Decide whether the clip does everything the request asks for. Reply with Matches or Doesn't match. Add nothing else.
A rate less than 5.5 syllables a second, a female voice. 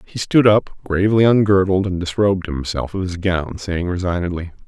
Doesn't match